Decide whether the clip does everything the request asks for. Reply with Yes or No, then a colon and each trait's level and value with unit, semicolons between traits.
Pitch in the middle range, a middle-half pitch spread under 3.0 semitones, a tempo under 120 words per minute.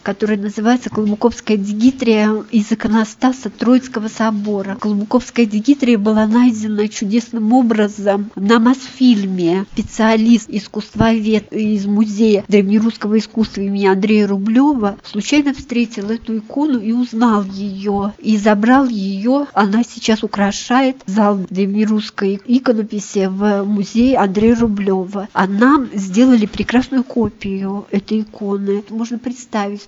No: high, 215 Hz; narrow, 2.6 semitones; slow, 110 wpm